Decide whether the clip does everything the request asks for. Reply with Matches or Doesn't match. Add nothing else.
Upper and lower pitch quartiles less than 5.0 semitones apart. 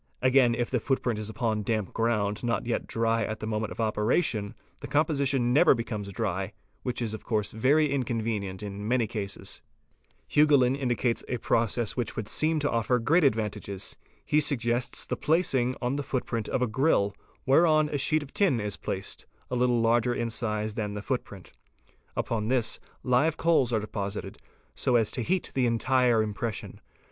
Matches